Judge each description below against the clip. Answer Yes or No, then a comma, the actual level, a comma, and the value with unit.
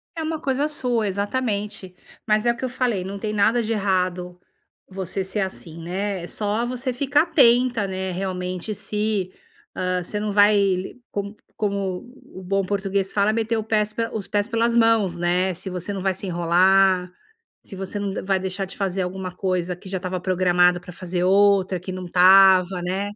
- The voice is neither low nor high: No, high, 195 Hz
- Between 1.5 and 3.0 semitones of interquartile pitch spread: Yes, narrow, 2.6 semitones